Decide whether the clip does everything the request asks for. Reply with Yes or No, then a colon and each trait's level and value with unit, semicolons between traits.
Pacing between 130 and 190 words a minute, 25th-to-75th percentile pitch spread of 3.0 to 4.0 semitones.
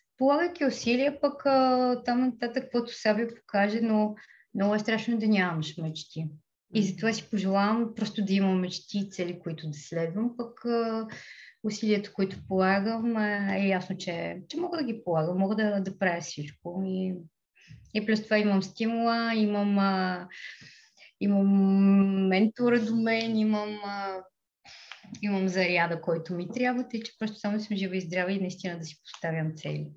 Yes: average, 160 wpm; average, 3.5 semitones